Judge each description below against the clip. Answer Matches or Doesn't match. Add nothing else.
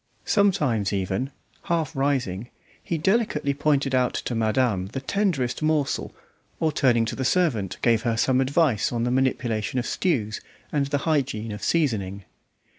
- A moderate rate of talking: Matches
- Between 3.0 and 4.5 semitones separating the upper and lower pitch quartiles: Doesn't match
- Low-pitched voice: Matches